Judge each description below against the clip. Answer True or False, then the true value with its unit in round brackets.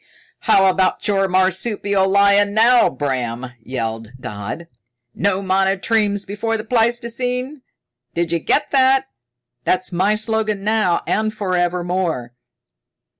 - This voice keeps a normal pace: False (115 wpm)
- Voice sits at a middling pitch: False (195 Hz)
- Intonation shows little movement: False (3.9 semitones)